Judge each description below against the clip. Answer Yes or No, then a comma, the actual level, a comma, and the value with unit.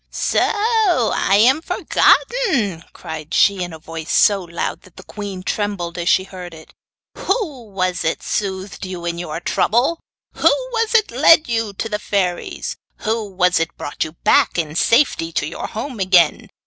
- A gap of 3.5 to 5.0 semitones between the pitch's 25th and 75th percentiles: Yes, average, 4.7 semitones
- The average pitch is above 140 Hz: Yes, high, 190 Hz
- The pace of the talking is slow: No, average, 170 wpm